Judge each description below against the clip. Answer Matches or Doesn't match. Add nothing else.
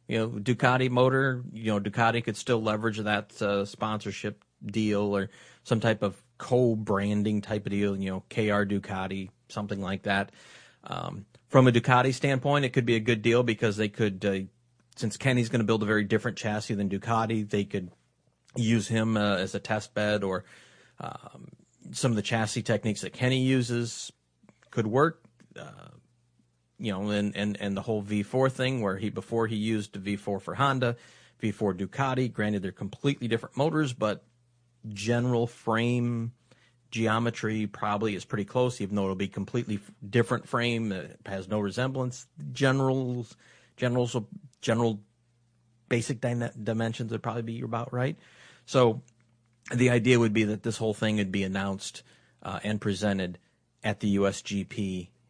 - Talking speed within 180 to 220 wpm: Doesn't match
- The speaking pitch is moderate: Doesn't match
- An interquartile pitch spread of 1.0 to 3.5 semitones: Matches